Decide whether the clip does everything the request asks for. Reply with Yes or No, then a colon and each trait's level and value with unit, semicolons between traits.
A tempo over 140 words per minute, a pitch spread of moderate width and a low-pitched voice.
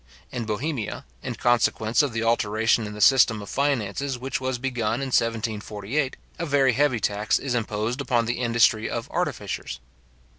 Yes: average, 160 wpm; average, 3.4 semitones; low, 115 Hz